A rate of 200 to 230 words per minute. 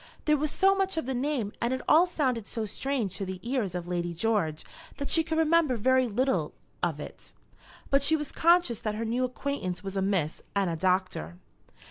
Yes: fast, 205 wpm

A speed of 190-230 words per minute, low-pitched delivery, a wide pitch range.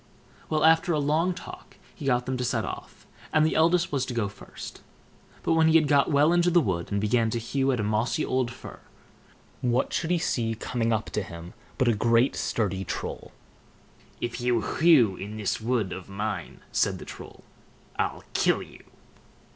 Yes: average, 195 wpm; low, 125 Hz; wide, 6.1 semitones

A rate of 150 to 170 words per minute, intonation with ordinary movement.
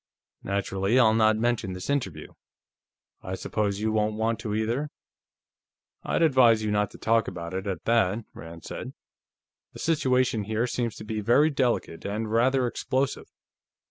Yes: average, 155 wpm; average, 3.2 semitones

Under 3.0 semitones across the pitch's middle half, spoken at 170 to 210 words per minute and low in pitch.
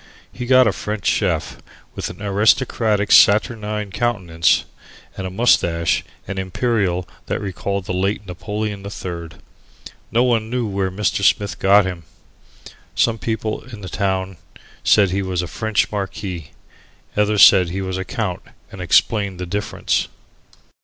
No: narrow, 2.5 semitones; average, 145 wpm; low, 100 Hz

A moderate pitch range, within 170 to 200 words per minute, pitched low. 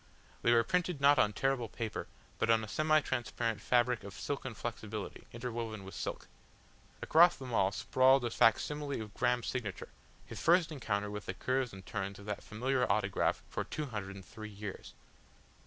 Yes: average, 4.2 semitones; average, 175 wpm; low, 115 Hz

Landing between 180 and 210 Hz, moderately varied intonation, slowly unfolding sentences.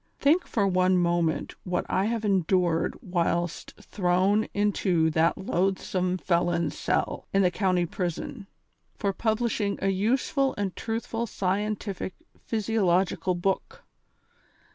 Yes: high, 190 Hz; average, 3.1 semitones; slow, 120 wpm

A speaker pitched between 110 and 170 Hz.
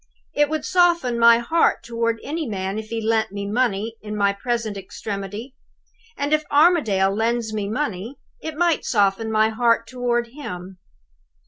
No: high, 230 Hz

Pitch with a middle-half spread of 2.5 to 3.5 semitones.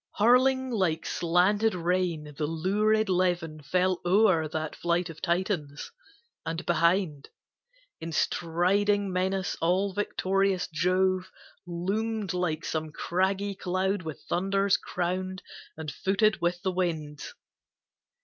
Yes: average, 2.8 semitones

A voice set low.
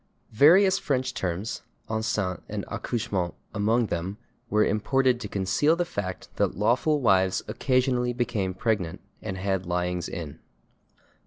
Yes: low, 105 Hz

